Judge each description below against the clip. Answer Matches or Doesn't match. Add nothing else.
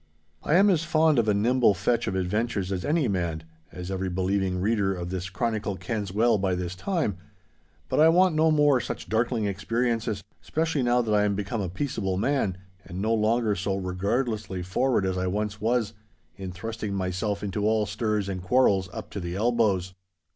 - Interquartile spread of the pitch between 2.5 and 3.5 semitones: Doesn't match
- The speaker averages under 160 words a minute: Doesn't match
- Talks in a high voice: Doesn't match